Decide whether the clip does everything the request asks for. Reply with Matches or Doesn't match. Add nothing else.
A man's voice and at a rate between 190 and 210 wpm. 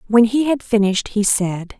Doesn't match